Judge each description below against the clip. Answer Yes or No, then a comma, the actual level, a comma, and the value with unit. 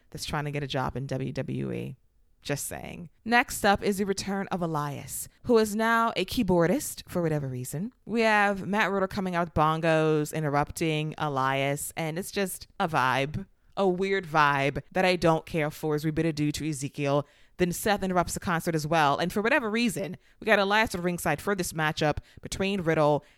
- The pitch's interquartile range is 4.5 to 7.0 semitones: Yes, average, 5.0 semitones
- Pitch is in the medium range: Yes, medium, 165 Hz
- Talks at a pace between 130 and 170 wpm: No, average, 190 wpm